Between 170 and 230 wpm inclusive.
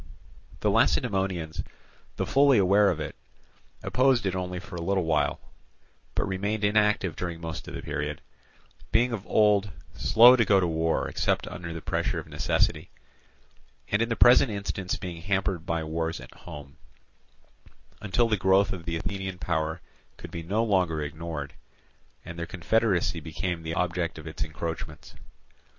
No: average, 160 wpm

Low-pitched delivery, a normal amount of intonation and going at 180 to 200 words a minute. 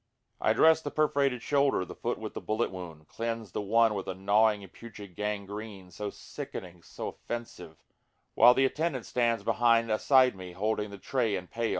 Yes: low, 110 Hz; average, 3.5 semitones; average, 185 wpm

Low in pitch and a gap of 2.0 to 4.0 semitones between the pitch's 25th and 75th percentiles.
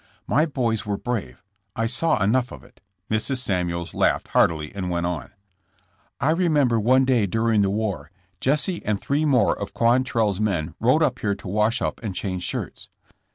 No: low, 110 Hz; average, 4.9 semitones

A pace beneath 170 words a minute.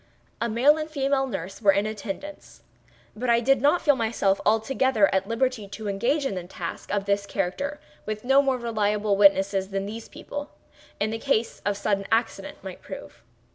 No: average, 180 wpm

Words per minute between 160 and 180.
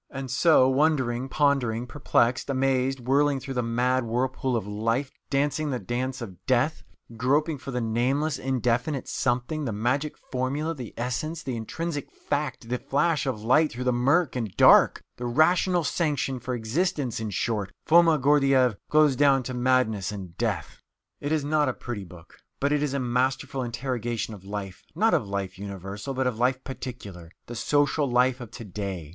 Yes: average, 175 wpm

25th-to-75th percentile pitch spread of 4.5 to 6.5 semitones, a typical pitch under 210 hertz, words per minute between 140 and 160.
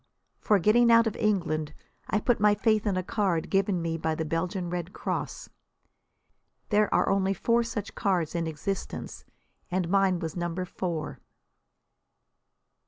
No: average, 3.8 semitones; medium, 185 Hz; average, 150 wpm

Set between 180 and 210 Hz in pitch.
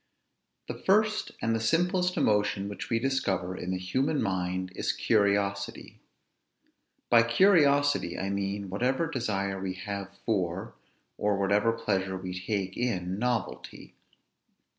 No: low, 100 Hz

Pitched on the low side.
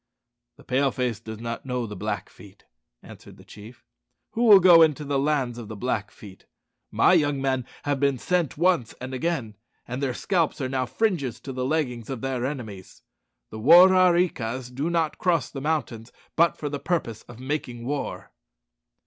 Yes: low, 130 Hz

